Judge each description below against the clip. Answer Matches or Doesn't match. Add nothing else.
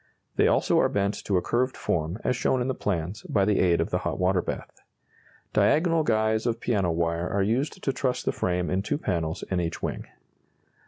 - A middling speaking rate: Doesn't match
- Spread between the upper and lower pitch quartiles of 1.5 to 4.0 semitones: Doesn't match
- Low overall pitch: Matches